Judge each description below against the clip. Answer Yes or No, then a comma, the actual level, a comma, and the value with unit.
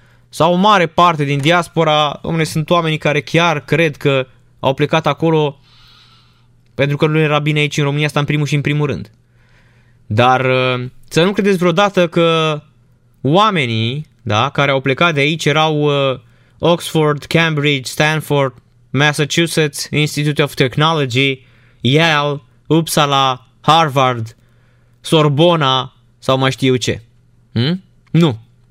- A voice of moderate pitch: Yes, medium, 145 Hz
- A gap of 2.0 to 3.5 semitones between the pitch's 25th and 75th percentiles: No, average, 4.1 semitones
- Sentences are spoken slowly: No, average, 130 wpm